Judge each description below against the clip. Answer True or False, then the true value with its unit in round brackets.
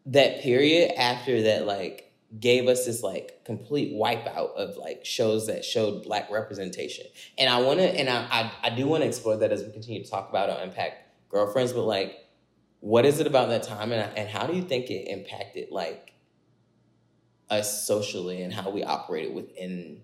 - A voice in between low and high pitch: False (120 Hz)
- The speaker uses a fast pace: False (190 wpm)